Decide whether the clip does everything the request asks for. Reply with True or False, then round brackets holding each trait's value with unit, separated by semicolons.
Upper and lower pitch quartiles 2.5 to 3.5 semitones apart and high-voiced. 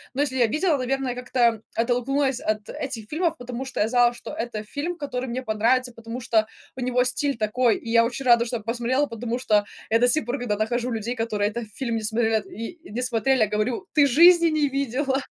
True (2.8 semitones; 245 Hz)